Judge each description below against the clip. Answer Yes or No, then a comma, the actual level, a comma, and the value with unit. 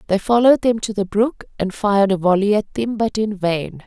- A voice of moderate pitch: No, high, 210 Hz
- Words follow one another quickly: Yes, fast, 235 wpm